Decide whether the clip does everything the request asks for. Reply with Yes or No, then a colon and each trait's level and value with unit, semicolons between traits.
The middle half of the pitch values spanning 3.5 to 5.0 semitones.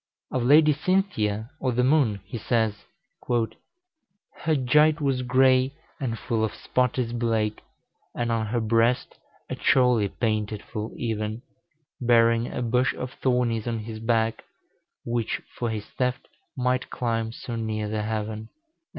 No: narrow, 2.5 semitones